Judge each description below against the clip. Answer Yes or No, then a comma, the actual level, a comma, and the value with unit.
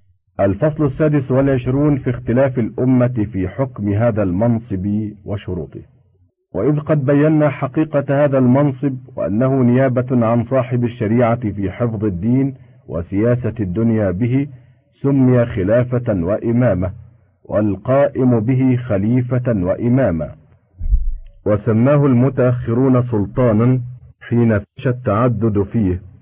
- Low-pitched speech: Yes, low, 120 Hz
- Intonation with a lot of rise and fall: No, average, 3.9 semitones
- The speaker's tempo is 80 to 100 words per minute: Yes, average, 95 wpm